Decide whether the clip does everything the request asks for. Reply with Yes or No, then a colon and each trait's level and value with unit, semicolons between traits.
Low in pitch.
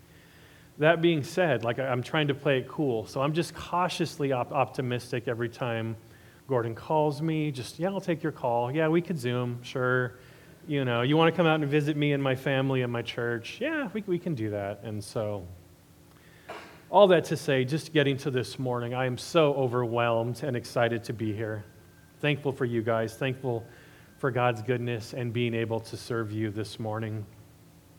Yes: low, 125 Hz